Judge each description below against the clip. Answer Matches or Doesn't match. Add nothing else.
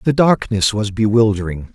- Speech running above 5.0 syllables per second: Doesn't match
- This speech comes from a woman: Doesn't match